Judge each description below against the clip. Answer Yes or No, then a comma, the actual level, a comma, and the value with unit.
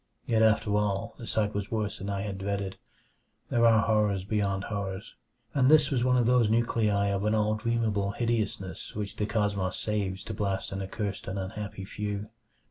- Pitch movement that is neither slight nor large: No, narrow, 2.0 semitones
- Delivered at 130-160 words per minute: No, average, 180 wpm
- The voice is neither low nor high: No, low, 105 Hz